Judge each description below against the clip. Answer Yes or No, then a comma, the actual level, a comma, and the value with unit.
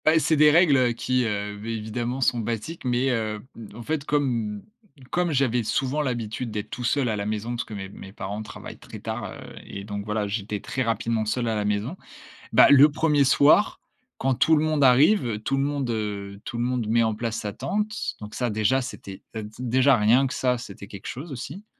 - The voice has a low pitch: Yes, low, 120 Hz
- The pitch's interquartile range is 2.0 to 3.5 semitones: No, average, 4.2 semitones